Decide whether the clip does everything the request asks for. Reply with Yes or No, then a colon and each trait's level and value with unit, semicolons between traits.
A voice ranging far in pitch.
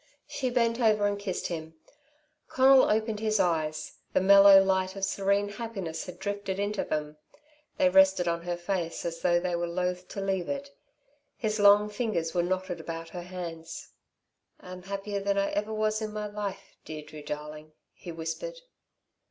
No: average, 3.3 semitones